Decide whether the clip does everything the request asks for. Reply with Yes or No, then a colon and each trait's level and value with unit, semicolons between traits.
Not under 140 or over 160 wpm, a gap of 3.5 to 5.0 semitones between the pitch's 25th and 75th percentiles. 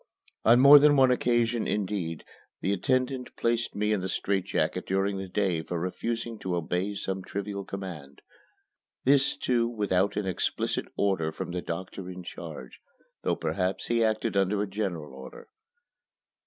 Yes: average, 155 wpm; average, 4.1 semitones